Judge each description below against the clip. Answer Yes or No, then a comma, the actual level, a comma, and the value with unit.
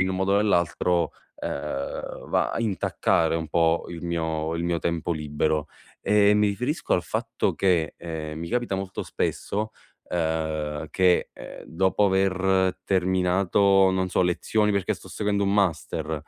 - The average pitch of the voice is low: Yes, very low, 90 Hz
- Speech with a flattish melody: No, average, 3.2 semitones